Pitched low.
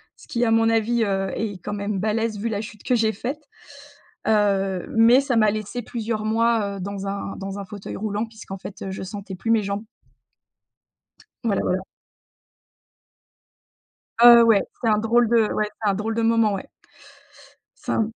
No: high, 215 Hz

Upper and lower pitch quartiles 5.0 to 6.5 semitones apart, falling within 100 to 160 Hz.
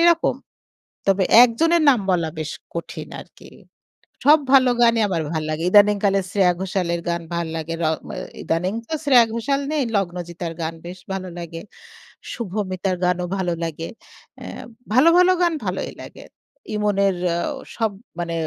No: average, 5.3 semitones; high, 190 Hz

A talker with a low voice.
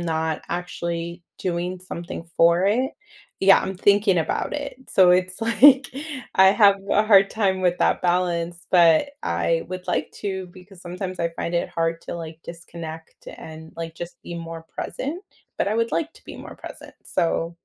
No: medium, 180 Hz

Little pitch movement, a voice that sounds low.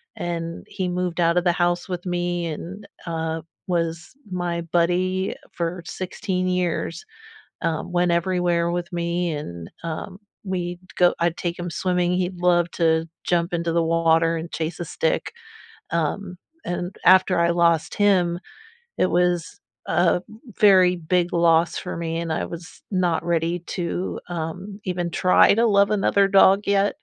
No: narrow, 1.4 semitones; medium, 175 Hz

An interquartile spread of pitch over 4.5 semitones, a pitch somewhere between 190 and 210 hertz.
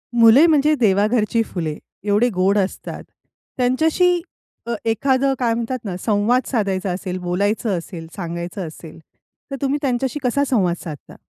No: wide, 5.4 semitones; high, 220 Hz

